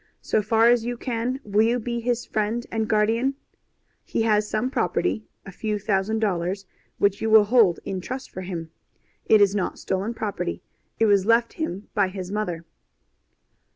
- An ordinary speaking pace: Yes, average, 175 wpm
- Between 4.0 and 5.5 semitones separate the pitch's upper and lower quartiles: No, average, 2.8 semitones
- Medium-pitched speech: No, high, 215 Hz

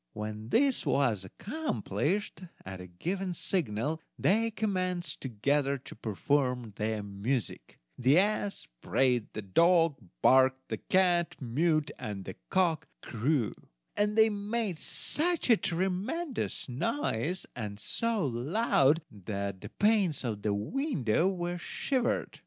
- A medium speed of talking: No, slow, 125 wpm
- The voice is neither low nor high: Yes, medium, 150 Hz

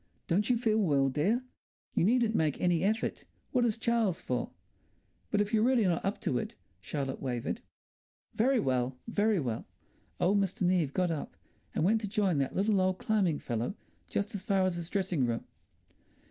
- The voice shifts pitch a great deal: Yes, wide, 5.9 semitones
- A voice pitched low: No, high, 190 Hz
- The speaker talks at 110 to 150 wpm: No, average, 180 wpm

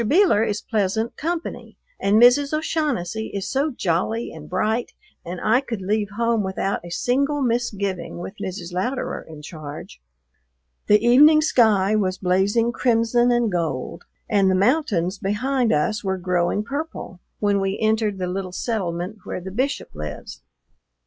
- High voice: Yes, high, 210 Hz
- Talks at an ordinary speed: Yes, average, 150 wpm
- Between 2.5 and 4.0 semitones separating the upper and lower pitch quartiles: No, average, 4.5 semitones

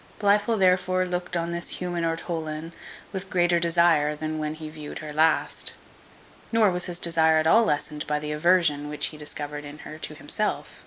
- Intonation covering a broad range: No, average, 2.7 semitones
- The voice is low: No, medium, 165 Hz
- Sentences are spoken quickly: No, average, 180 wpm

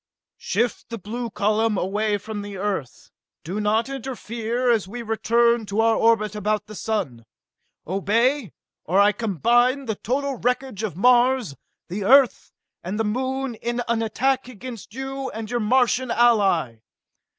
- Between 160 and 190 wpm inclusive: No, average, 150 wpm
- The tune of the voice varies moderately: Yes, average, 3.0 semitones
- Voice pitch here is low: No, high, 225 Hz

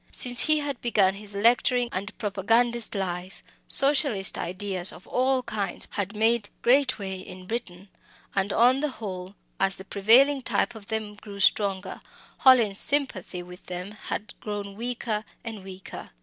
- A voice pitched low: No, high, 210 Hz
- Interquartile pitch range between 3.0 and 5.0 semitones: Yes, average, 3.9 semitones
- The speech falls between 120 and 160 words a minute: Yes, average, 150 wpm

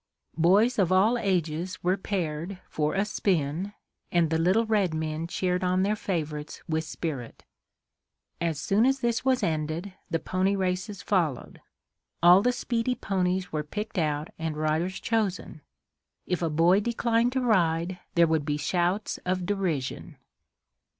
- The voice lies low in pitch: No, medium, 180 Hz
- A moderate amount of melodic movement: Yes, average, 3.9 semitones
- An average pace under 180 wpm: Yes, average, 150 wpm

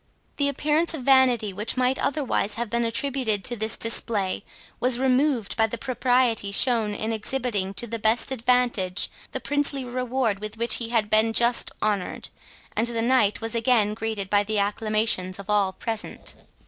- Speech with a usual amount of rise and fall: Yes, average, 3.1 semitones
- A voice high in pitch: Yes, high, 230 Hz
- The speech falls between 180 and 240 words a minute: No, average, 170 wpm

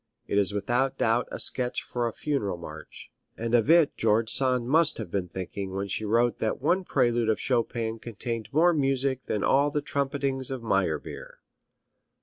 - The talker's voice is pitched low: Yes, low, 120 Hz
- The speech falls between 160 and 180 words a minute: Yes, average, 175 wpm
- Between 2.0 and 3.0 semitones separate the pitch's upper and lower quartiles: No, average, 4.3 semitones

